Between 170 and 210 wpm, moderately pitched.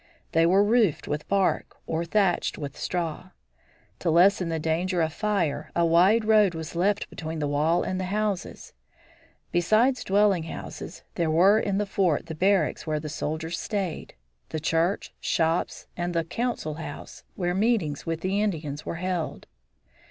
No: average, 160 wpm; medium, 175 Hz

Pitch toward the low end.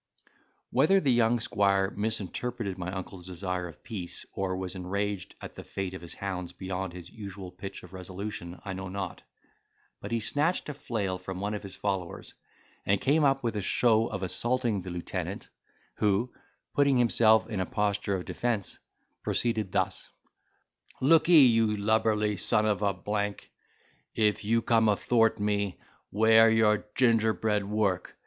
Yes: low, 105 Hz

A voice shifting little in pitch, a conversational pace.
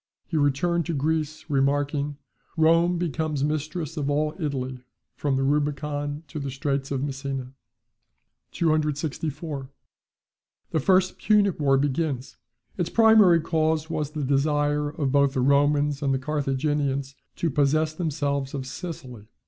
No: narrow, 2.3 semitones; slow, 130 wpm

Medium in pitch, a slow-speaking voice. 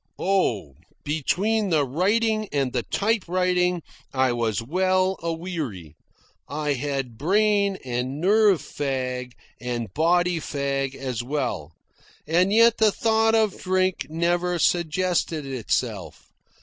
Yes: medium, 165 Hz; slow, 115 wpm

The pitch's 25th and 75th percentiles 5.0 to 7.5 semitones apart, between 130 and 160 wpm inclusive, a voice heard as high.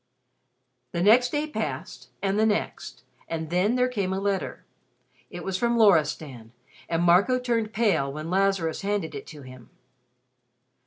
Yes: wide, 5.4 semitones; average, 150 wpm; high, 195 Hz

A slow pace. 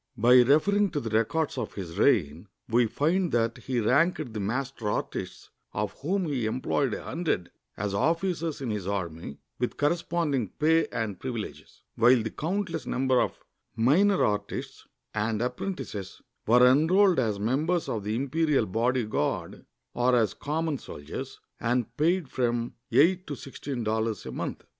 No: average, 150 wpm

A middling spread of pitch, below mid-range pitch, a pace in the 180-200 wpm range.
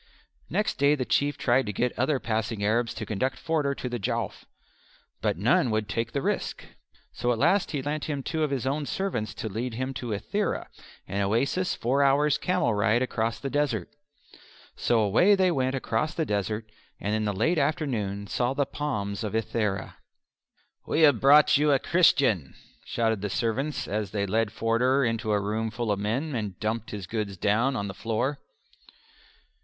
Yes: average, 4.8 semitones; low, 120 Hz; average, 185 wpm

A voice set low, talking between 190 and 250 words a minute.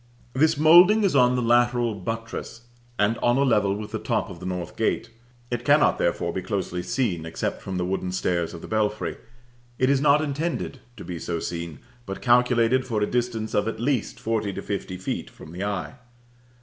Yes: low, 115 Hz; average, 200 wpm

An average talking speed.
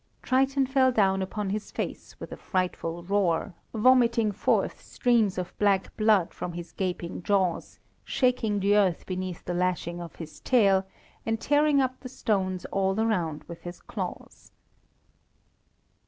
Yes: average, 145 wpm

